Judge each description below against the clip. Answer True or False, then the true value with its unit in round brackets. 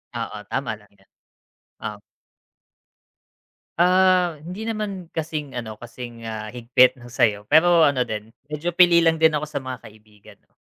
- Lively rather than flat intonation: True (7.0 semitones)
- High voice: False (140 Hz)